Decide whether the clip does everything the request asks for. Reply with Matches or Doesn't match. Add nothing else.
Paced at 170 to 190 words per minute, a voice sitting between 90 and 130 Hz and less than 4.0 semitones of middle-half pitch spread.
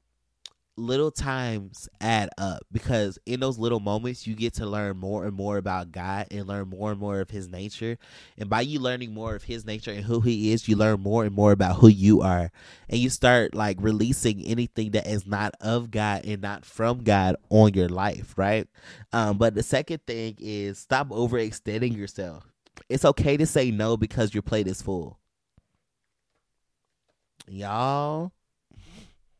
Matches